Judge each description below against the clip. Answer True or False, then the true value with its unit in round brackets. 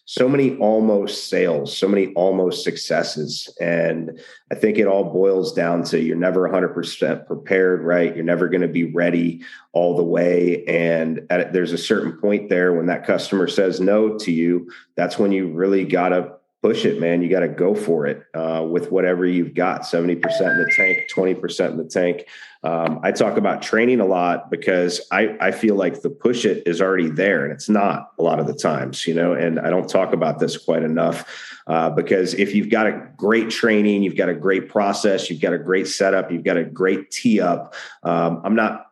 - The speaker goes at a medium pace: False (210 wpm)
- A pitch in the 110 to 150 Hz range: False (90 Hz)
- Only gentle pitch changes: True (2.1 semitones)